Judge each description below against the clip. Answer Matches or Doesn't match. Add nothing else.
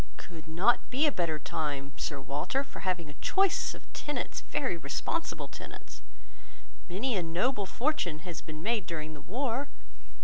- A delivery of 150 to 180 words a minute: Matches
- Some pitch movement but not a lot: Doesn't match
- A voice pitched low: Doesn't match